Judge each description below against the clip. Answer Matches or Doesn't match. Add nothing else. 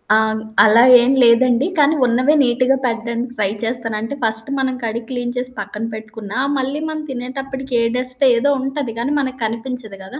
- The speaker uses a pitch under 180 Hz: Doesn't match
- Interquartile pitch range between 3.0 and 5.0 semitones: Doesn't match